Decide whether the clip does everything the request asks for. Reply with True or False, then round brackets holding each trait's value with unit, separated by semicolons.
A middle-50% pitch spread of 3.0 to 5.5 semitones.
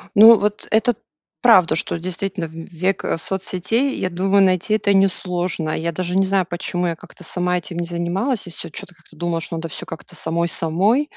False (2.6 semitones)